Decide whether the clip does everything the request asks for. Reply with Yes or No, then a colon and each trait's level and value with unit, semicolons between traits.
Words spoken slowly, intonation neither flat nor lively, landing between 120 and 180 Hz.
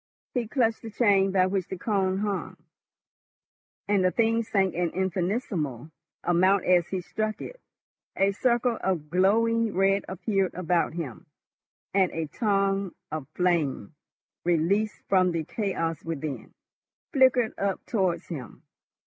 No: slow, 130 wpm; average, 3.5 semitones; high, 190 Hz